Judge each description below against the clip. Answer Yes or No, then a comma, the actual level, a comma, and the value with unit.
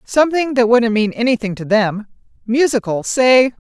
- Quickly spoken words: No, average, 145 wpm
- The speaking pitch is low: No, high, 235 Hz